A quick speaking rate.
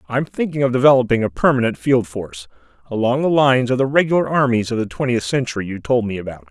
Yes: fast, 210 wpm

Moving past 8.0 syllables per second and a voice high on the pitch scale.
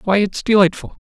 No: 5.6 syllables/s; high, 200 Hz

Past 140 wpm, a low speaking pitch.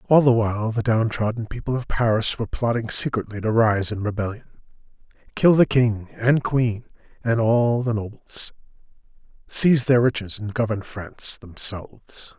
Yes: average, 150 wpm; low, 115 Hz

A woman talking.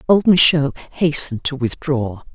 Yes: female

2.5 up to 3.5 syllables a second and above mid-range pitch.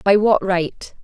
Yes: 3.4 syllables/s; high, 195 Hz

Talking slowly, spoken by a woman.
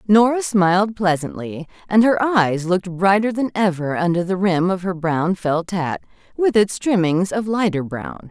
No: average, 175 wpm; female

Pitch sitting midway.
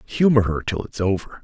No: low, 105 Hz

